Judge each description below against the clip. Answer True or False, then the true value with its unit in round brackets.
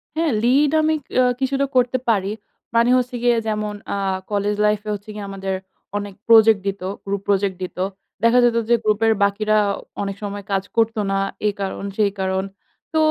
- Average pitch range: True (3.0 semitones)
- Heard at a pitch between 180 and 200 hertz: False (210 Hz)